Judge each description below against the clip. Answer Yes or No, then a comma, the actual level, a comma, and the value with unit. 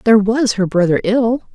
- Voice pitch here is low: No, high, 215 Hz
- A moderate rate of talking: Yes, average, 195 wpm